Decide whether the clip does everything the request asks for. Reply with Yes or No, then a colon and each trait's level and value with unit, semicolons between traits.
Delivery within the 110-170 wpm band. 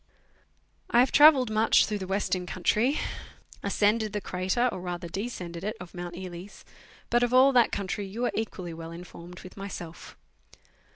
Yes: average, 165 wpm